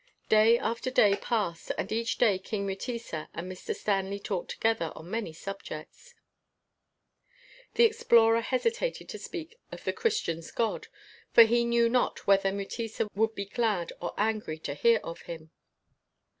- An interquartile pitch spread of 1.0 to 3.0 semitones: No, average, 3.5 semitones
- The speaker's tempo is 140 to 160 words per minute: Yes, average, 150 wpm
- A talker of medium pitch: No, high, 220 Hz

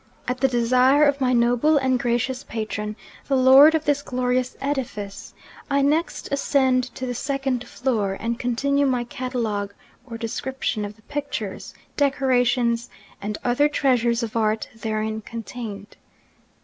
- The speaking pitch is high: Yes, very high, 250 Hz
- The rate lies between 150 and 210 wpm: No, average, 140 wpm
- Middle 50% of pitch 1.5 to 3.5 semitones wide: Yes, average, 2.9 semitones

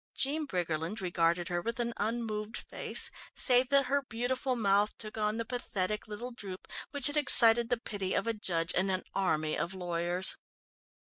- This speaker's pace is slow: No, average, 175 wpm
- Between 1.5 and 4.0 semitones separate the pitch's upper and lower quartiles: No, average, 4.8 semitones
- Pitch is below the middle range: No, high, 215 Hz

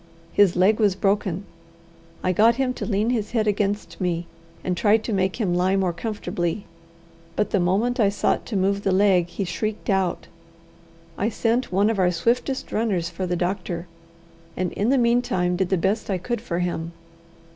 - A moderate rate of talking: Yes, average, 185 wpm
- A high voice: Yes, high, 195 Hz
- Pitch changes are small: No, average, 3.3 semitones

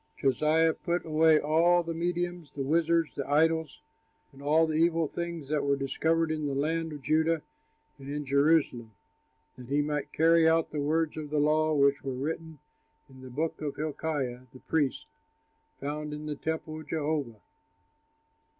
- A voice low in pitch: No, medium, 155 Hz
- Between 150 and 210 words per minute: Yes, average, 170 wpm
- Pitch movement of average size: No, narrow, 2.3 semitones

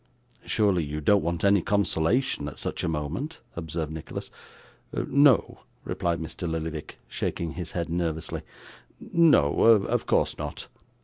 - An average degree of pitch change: Yes, average, 4.3 semitones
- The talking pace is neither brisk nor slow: No, slow, 130 wpm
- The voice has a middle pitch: No, very low, 85 Hz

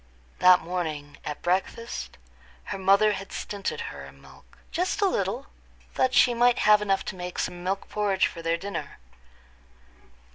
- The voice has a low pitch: No, high, 195 Hz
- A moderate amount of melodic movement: Yes, average, 3.0 semitones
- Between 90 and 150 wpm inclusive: Yes, average, 145 wpm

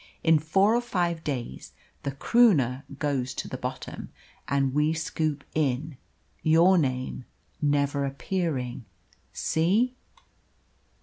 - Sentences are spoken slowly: Yes, slow, 110 wpm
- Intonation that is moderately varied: Yes, average, 3.7 semitones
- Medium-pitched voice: Yes, medium, 150 Hz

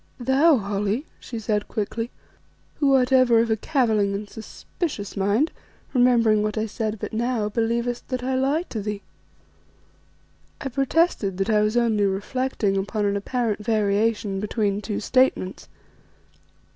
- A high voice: Yes, high, 220 Hz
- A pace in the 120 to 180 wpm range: Yes, average, 145 wpm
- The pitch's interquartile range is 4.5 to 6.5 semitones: No, average, 3.4 semitones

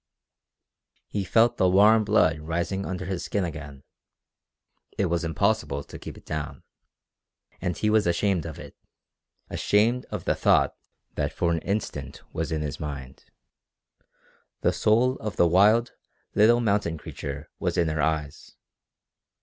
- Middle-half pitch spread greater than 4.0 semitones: Yes, average, 5.2 semitones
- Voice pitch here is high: No, very low, 90 Hz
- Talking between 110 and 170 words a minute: Yes, average, 145 wpm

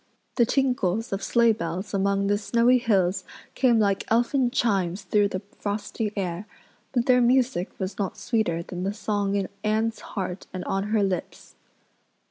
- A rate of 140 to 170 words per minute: Yes, average, 160 wpm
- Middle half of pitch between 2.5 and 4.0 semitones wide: Yes, average, 3.4 semitones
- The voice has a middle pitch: No, high, 205 Hz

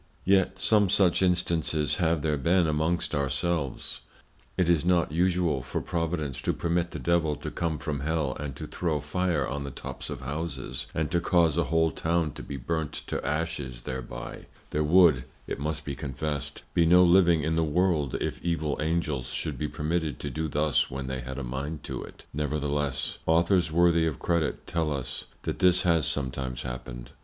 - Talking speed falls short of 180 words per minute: No, average, 185 wpm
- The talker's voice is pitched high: No, very low, 80 Hz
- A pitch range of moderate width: Yes, average, 3.5 semitones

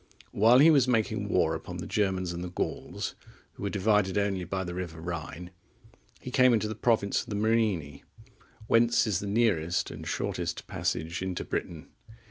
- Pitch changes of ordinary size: Yes, average, 4.1 semitones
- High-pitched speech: No, low, 100 Hz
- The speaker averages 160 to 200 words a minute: Yes, average, 175 wpm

